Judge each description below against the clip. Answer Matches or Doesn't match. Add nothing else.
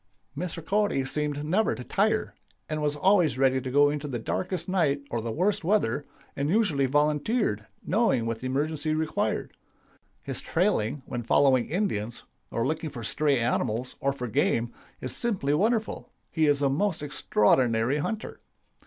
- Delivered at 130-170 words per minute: Matches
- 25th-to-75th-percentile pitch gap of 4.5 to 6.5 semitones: Matches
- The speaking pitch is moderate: Matches